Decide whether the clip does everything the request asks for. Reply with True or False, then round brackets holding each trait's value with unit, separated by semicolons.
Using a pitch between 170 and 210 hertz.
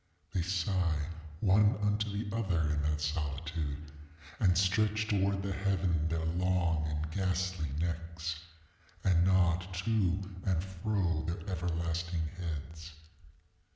False (85 Hz)